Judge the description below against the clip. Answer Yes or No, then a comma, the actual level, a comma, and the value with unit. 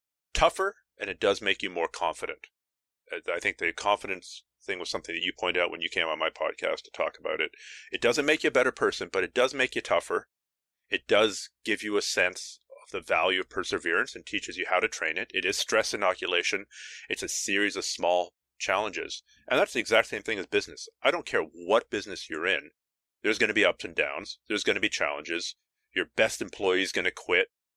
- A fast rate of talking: Yes, fast, 225 wpm